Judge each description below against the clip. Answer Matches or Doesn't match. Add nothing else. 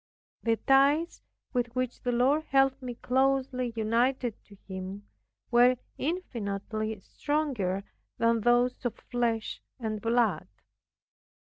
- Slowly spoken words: Matches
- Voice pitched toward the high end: Matches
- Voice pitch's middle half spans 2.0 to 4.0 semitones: Matches